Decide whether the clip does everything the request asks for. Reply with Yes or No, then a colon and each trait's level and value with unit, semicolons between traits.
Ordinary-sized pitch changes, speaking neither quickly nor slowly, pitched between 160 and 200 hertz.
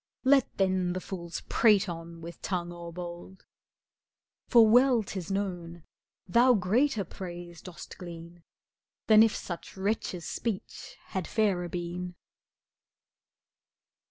No: average, 3.6 semitones; slow, 110 wpm; medium, 185 Hz